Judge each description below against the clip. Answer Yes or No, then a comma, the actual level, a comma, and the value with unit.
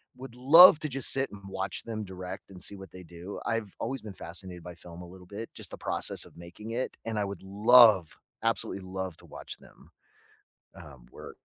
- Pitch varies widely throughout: No, average, 4.0 semitones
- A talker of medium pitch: No, low, 100 Hz